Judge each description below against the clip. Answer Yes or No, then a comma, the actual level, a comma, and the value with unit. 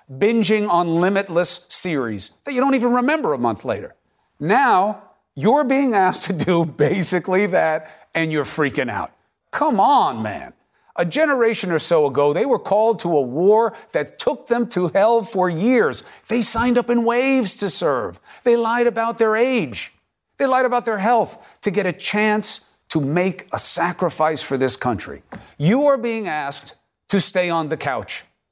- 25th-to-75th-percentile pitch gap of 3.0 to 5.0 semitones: No, wide, 5.6 semitones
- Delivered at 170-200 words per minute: Yes, average, 175 wpm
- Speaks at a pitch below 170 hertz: No, high, 205 Hz